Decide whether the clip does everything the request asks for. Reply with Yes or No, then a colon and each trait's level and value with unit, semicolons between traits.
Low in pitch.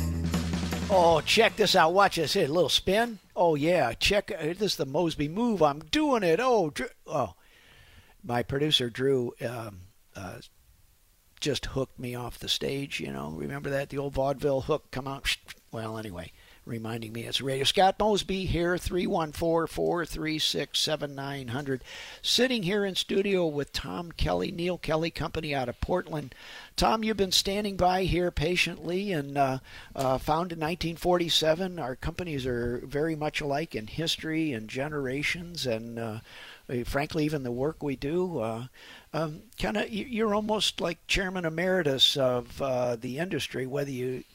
No: medium, 150 Hz